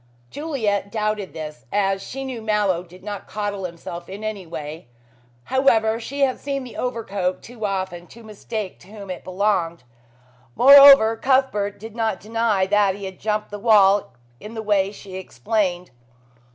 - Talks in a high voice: Yes, high, 205 Hz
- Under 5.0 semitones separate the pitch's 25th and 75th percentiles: Yes, average, 3.0 semitones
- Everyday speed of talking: Yes, average, 160 wpm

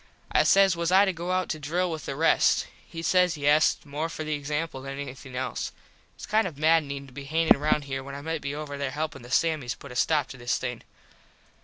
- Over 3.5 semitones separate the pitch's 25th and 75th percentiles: No, average, 3.0 semitones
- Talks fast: Yes, fast, 235 wpm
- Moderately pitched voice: Yes, medium, 150 Hz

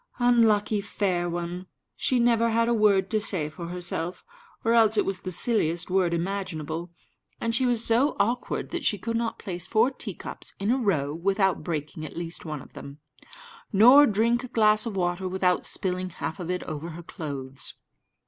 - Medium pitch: No, high, 195 Hz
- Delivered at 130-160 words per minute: No, average, 185 wpm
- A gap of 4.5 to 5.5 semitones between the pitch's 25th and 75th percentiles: Yes, average, 4.8 semitones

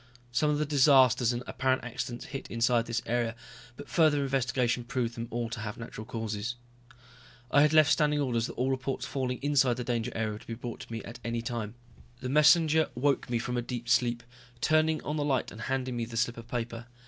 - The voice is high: No, low, 125 Hz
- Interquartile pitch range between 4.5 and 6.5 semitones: No, average, 3.0 semitones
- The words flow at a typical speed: No, fast, 220 wpm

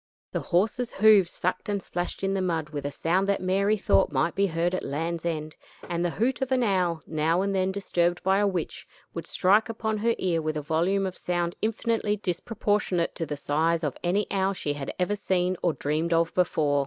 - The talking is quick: Yes, fast, 215 wpm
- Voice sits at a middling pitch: Yes, medium, 180 Hz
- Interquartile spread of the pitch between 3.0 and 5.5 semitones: Yes, average, 3.4 semitones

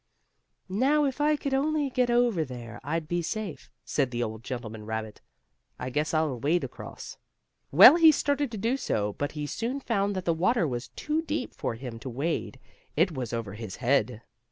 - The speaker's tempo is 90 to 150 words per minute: No, average, 190 wpm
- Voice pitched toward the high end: No, medium, 160 Hz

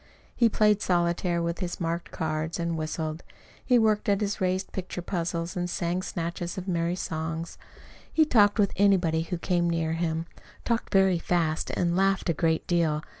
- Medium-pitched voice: Yes, medium, 175 Hz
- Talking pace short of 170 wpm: No, average, 175 wpm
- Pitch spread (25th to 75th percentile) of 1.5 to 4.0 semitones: Yes, narrow, 2.5 semitones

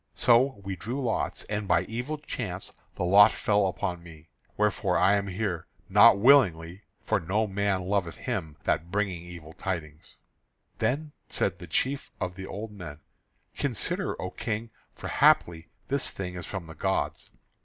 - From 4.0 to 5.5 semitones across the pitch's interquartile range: No, average, 3.6 semitones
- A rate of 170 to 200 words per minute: No, average, 160 wpm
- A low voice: Yes, very low, 95 Hz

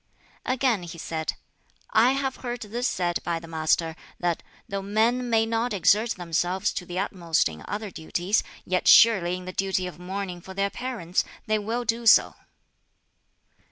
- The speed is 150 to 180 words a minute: Yes, average, 165 wpm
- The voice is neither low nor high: No, high, 195 Hz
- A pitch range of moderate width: Yes, average, 4.5 semitones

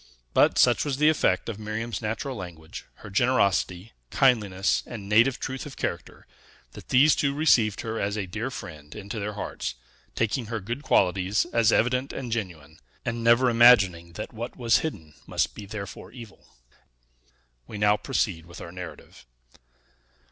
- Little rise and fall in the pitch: No, average, 4.1 semitones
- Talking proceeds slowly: No, average, 160 wpm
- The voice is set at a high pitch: No, low, 110 Hz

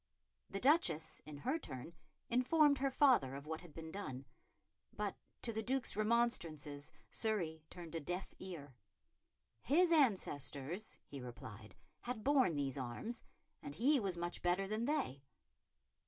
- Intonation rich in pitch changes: Yes, wide, 8.7 semitones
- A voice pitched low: No, medium, 185 Hz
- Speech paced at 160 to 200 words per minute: No, average, 140 wpm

